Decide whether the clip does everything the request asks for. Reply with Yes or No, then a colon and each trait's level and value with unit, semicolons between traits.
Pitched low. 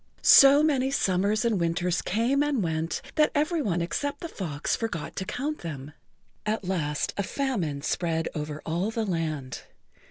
No: high, 190 Hz